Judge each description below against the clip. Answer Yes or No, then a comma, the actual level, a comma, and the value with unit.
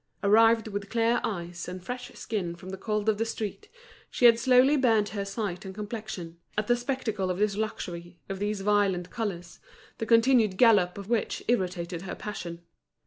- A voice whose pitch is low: No, high, 205 Hz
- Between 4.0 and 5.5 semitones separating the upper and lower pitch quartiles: No, average, 3.6 semitones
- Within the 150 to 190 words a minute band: Yes, average, 180 wpm